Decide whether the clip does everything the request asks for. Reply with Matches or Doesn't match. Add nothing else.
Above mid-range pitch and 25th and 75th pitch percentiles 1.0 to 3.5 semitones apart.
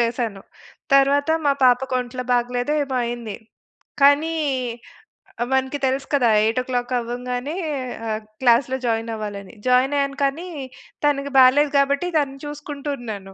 Matches